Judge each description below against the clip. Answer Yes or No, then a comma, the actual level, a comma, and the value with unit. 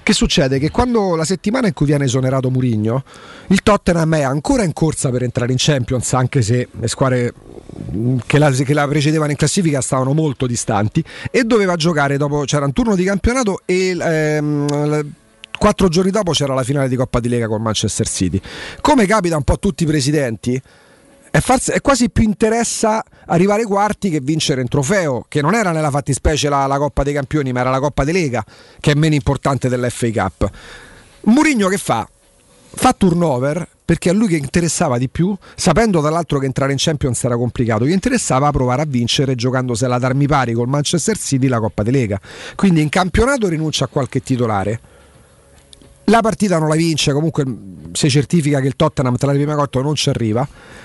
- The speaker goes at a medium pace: No, fast, 190 wpm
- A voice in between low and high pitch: Yes, medium, 145 Hz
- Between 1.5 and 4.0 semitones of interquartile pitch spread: No, wide, 5.4 semitones